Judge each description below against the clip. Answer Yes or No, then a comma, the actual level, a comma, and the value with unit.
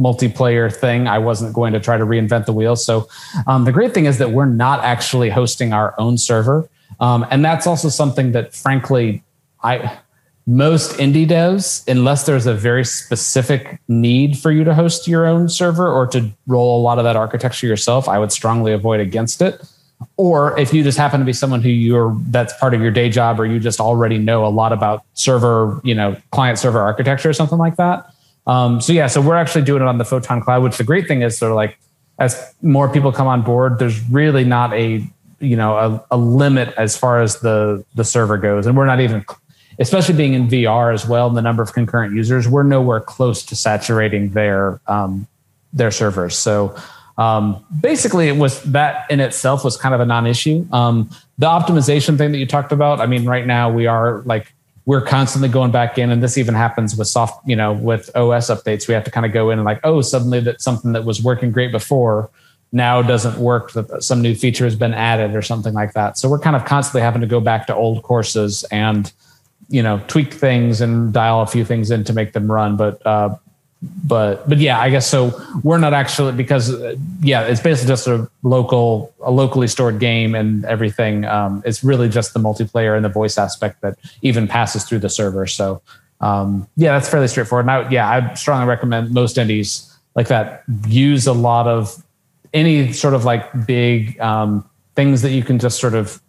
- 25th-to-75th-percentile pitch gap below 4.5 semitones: Yes, average, 3.3 semitones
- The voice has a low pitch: Yes, low, 120 Hz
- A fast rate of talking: Yes, fast, 215 wpm